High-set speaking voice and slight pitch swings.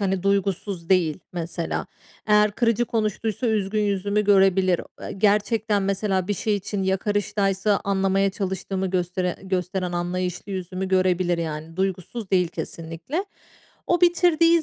Yes: high, 195 Hz; narrow, 2.3 semitones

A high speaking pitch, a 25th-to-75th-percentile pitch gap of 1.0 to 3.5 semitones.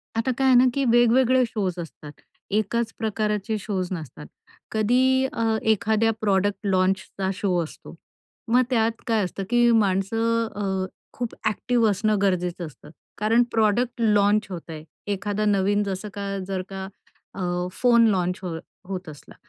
Yes: high, 210 Hz; average, 3.2 semitones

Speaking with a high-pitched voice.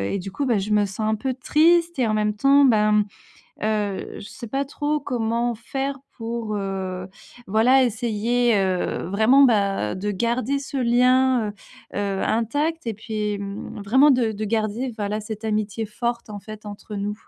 Yes: high, 220 Hz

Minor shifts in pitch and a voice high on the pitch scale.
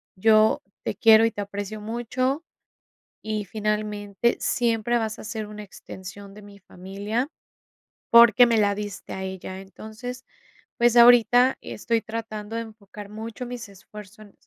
Yes: narrow, 2.2 semitones; high, 215 Hz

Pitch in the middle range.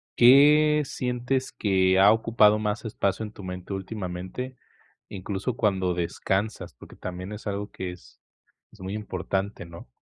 No: low, 100 Hz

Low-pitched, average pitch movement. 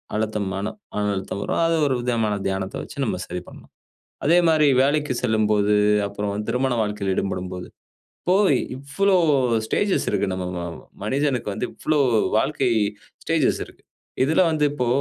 No: low, 110 Hz; wide, 5.9 semitones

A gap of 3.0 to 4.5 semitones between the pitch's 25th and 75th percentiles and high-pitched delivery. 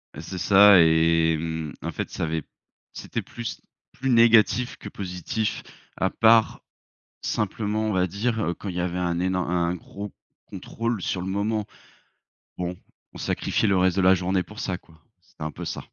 No: average, 3.5 semitones; very low, 95 Hz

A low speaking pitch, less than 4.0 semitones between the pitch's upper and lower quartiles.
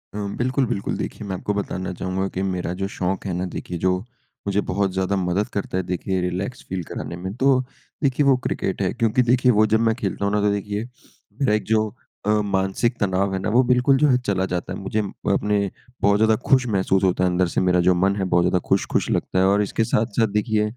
Yes: low, 100 Hz; average, 2.9 semitones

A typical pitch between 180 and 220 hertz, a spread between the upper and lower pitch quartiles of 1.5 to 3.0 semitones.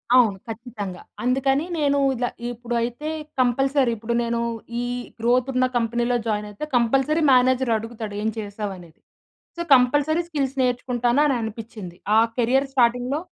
No: high, 245 Hz; average, 2.7 semitones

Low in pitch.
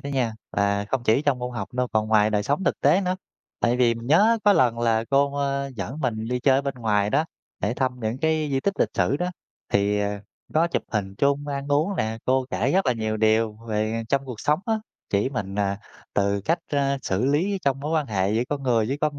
Yes: low, 125 Hz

